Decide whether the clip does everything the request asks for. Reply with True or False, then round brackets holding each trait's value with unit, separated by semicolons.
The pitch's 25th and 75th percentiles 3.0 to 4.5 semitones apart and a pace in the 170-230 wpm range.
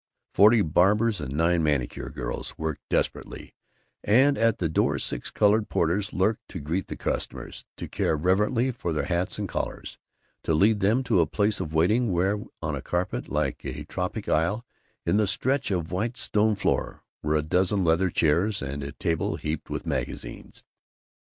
False (4.9 semitones; 175 wpm)